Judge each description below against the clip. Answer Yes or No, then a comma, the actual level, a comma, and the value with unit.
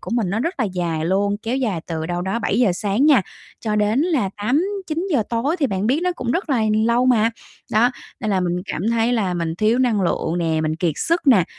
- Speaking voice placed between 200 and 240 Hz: Yes, high, 220 Hz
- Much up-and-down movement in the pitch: Yes, wide, 5.9 semitones